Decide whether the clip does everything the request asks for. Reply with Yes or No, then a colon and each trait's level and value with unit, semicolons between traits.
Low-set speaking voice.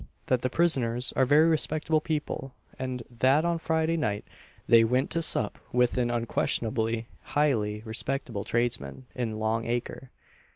Yes: low, 125 Hz